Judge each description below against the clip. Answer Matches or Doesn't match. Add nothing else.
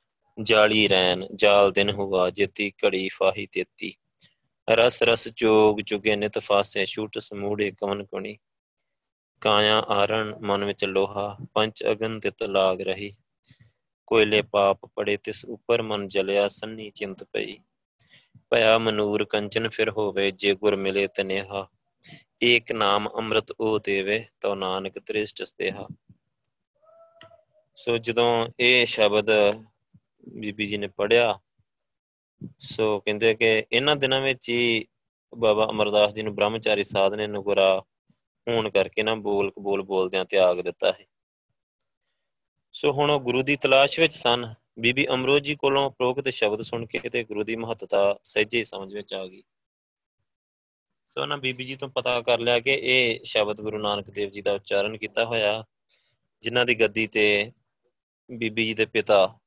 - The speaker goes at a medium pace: Matches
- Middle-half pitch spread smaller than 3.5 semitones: Matches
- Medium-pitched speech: Doesn't match